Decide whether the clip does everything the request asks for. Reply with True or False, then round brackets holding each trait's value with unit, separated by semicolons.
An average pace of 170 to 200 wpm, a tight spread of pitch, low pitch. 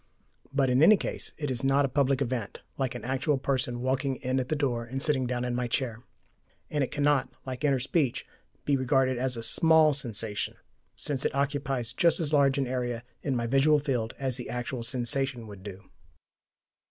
True (195 wpm; 2.3 semitones; 130 Hz)